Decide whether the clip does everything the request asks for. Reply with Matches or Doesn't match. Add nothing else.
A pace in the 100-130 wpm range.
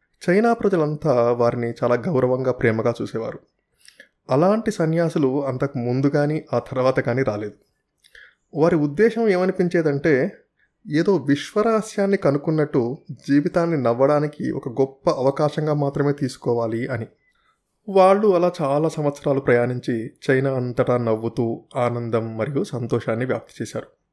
Matches